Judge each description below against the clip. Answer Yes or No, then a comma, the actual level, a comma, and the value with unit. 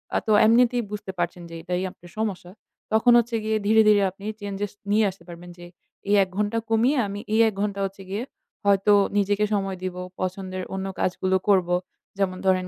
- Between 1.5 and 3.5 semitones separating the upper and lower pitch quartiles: Yes, narrow, 2.4 semitones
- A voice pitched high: Yes, high, 200 Hz